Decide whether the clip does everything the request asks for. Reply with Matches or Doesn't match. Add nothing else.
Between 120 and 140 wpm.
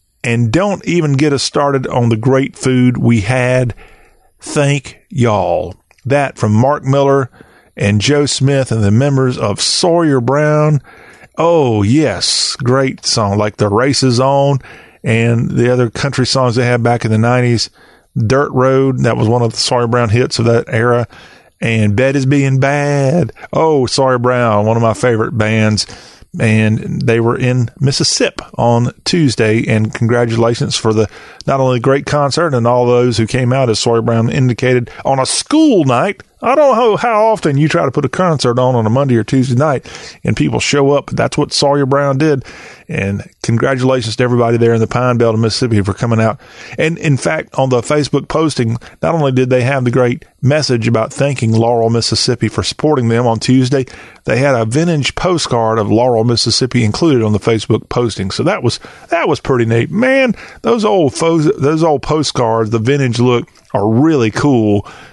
Doesn't match